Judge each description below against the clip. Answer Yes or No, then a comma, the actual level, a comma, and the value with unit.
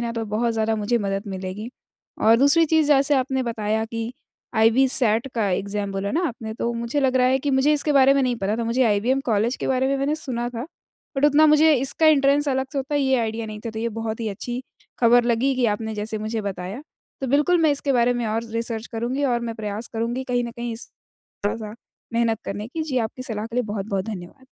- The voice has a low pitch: No, high, 235 Hz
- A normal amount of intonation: Yes, average, 3.3 semitones